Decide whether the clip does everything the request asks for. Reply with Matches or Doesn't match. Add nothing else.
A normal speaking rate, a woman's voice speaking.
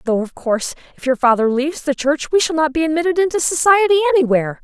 Doesn't match